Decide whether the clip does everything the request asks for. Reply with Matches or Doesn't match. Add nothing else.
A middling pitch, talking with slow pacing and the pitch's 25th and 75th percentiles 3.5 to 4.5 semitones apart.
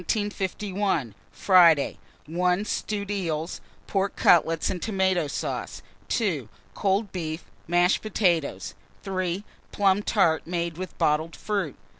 Doesn't match